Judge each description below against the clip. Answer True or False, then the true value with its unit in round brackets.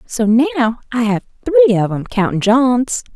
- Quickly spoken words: False (170 wpm)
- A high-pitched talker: True (230 Hz)